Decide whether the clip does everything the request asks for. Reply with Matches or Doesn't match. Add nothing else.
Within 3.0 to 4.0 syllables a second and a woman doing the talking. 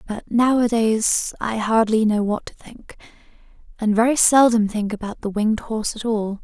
Doesn't match